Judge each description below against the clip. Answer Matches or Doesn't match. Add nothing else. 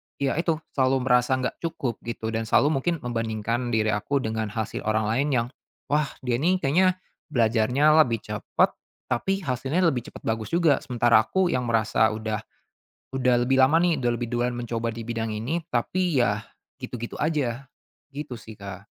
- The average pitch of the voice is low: Matches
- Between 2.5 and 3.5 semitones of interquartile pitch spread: Doesn't match